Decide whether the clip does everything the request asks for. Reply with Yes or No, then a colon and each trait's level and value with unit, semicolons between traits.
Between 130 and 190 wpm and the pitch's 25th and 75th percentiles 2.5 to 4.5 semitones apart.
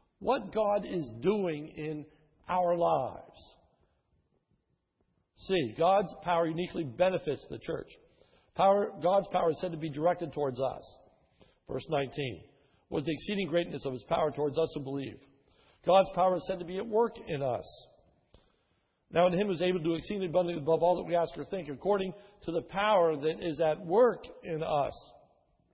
Yes: average, 170 wpm; average, 3.8 semitones